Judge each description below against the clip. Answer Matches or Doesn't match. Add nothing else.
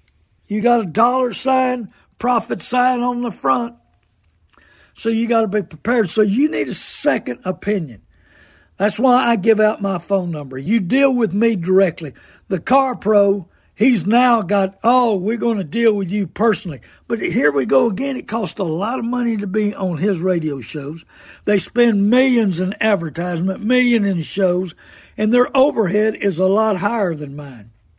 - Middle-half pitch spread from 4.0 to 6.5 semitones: Matches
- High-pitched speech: Matches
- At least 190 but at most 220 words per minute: Doesn't match